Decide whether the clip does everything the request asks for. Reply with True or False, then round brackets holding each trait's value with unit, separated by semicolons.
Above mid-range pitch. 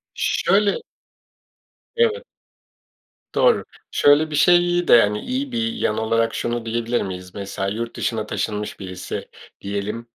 False (115 Hz)